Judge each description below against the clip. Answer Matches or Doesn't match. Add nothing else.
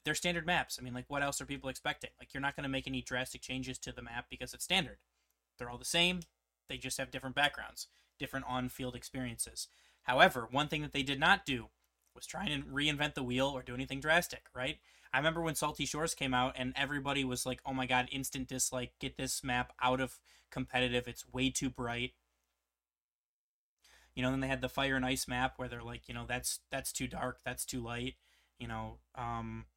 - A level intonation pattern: Matches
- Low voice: Matches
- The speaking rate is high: Matches